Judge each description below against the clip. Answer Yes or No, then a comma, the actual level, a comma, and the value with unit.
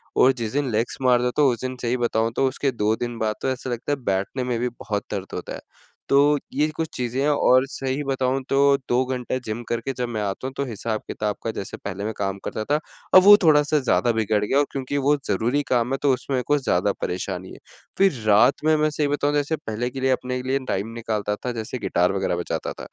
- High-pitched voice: No, low, 125 Hz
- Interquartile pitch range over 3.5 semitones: Yes, average, 3.9 semitones